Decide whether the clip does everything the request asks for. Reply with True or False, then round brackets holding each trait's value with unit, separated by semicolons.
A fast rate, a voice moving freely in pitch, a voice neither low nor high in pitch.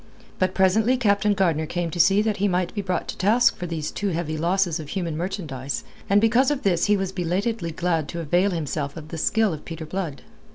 False (220 wpm; 3.7 semitones; 180 Hz)